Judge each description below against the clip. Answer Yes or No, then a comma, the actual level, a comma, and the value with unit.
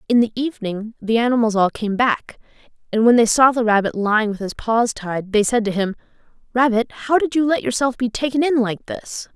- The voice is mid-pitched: No, high, 230 Hz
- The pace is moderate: No, fast, 220 wpm